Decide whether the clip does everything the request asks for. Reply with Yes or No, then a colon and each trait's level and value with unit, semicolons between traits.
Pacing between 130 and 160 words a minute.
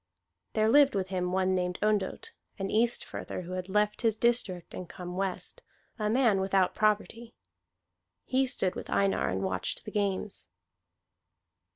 Yes: average, 150 wpm